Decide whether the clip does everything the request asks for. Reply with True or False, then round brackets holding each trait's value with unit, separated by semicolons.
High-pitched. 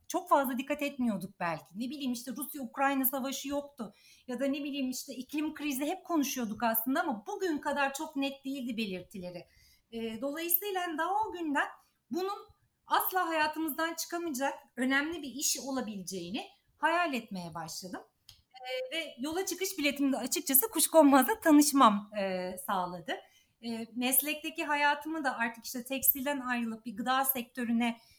True (275 Hz)